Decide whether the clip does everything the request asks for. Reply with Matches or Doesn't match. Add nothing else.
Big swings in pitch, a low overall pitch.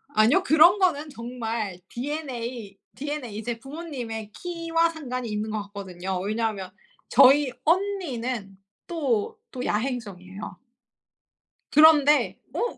Doesn't match